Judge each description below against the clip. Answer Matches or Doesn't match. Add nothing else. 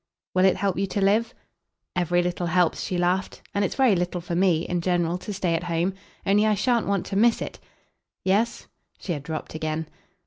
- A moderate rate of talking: Doesn't match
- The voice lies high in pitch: Doesn't match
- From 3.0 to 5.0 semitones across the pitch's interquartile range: Doesn't match